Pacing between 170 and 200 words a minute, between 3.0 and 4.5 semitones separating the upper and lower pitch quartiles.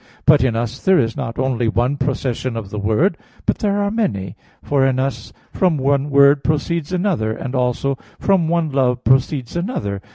No: average, 185 wpm; average, 5.0 semitones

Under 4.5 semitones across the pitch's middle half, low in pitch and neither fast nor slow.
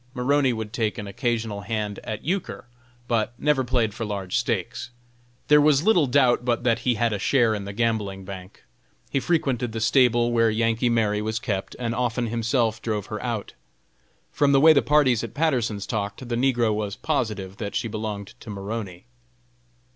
Yes: average, 2.9 semitones; low, 115 Hz; average, 180 wpm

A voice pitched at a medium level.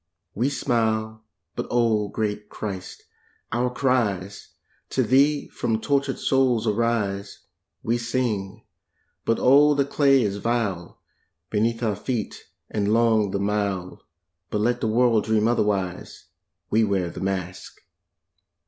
No: low, 110 Hz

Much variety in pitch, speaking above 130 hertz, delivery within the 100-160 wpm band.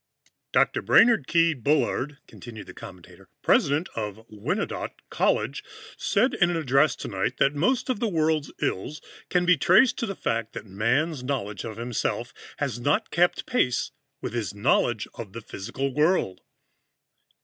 Yes: wide, 6.6 semitones; medium, 140 Hz; average, 150 wpm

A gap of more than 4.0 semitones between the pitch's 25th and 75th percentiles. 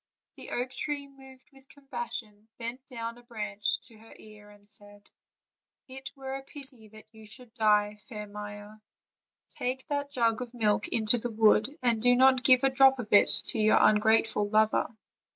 No: average, 3.5 semitones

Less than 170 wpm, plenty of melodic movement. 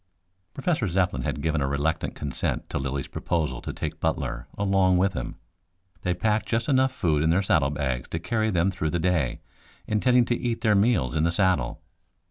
No: average, 190 wpm; wide, 6.3 semitones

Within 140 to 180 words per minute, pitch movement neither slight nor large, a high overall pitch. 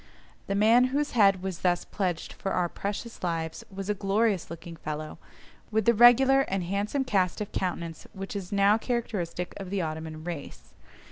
Yes: average, 175 wpm; average, 3.8 semitones; high, 195 Hz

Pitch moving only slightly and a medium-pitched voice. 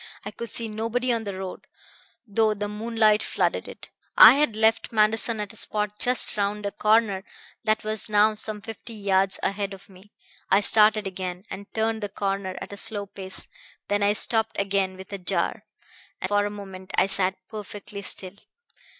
No: narrow, 1.9 semitones; high, 205 Hz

